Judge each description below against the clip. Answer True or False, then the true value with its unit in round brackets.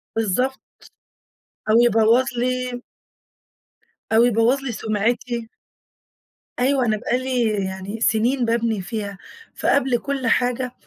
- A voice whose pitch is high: True (240 Hz)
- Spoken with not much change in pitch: True (2.3 semitones)